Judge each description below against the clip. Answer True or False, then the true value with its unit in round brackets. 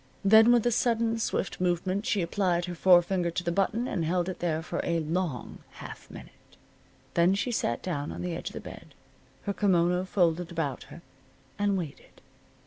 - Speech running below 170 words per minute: False (185 wpm)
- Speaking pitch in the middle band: True (180 Hz)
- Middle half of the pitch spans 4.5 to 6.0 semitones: False (2.9 semitones)